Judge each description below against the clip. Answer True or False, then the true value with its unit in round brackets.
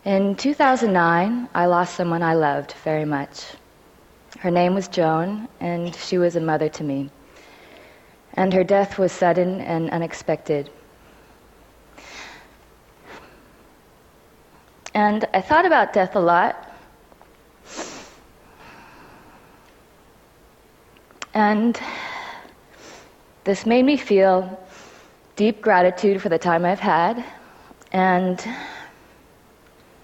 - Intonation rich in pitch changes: False (3.7 semitones)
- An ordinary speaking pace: False (95 wpm)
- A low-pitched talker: False (185 Hz)